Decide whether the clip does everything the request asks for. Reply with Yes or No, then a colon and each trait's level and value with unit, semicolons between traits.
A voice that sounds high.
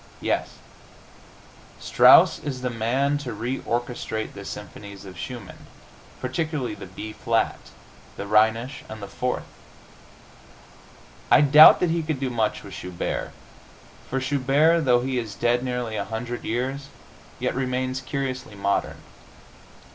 No: low, 125 Hz